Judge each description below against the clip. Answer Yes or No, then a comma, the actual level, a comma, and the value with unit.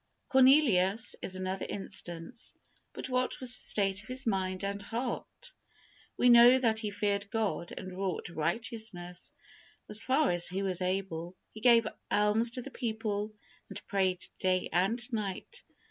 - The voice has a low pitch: No, high, 205 Hz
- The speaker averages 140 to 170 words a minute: Yes, average, 150 wpm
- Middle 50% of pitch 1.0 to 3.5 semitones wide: No, average, 3.9 semitones